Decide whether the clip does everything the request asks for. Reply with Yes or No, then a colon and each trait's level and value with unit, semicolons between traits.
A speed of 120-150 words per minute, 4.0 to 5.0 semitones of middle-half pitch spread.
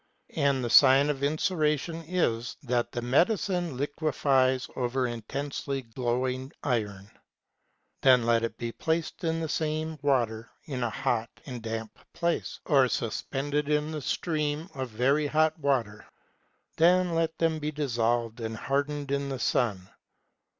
Yes: average, 140 wpm; average, 4.3 semitones